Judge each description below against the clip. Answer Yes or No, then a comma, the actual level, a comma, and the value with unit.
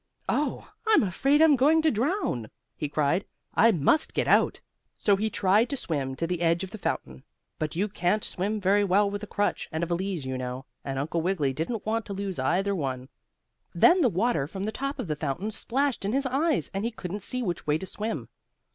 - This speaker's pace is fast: Yes, fast, 220 wpm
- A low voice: No, high, 195 Hz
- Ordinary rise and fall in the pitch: No, wide, 6.1 semitones